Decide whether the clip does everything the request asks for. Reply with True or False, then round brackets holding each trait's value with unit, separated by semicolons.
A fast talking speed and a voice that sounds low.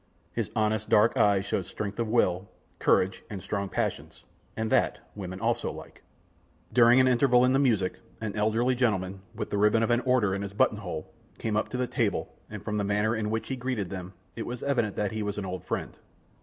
True (215 wpm; 105 Hz)